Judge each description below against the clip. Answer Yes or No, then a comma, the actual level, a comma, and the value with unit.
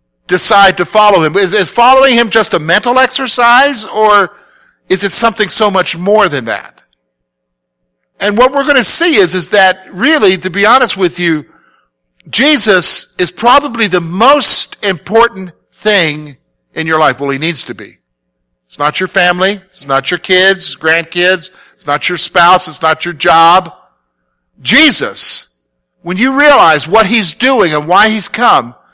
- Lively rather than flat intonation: Yes, wide, 5.9 semitones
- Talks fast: No, average, 165 wpm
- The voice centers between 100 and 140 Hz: No, medium, 185 Hz